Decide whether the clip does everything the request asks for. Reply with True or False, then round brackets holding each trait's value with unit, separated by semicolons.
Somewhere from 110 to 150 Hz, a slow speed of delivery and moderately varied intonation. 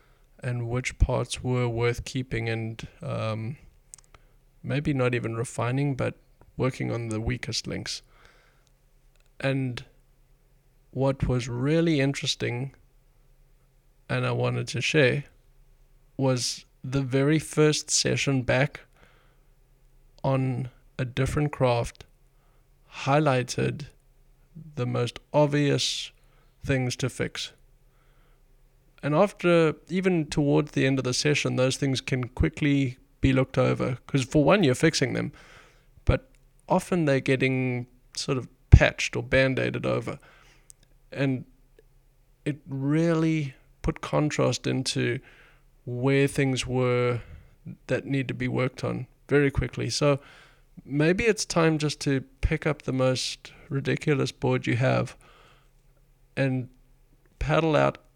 False (135 Hz; 115 wpm; 1.8 semitones)